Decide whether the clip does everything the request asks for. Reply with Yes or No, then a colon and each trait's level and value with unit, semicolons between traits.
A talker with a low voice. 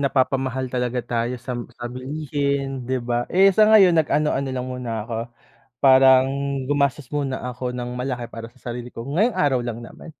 Yes: low, 130 Hz